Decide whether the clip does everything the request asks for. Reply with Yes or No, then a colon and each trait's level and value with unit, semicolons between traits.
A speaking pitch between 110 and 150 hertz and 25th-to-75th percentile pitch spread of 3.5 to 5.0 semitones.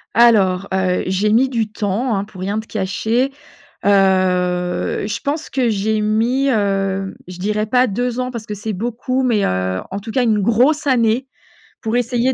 No: high, 215 Hz; average, 4.0 semitones